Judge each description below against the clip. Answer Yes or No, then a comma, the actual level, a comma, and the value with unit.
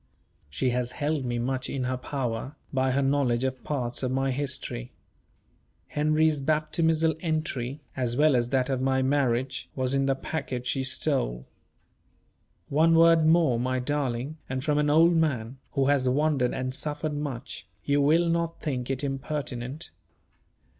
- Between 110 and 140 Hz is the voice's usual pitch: Yes, low, 135 Hz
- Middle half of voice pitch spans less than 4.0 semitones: Yes, average, 3.0 semitones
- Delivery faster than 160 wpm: No, average, 155 wpm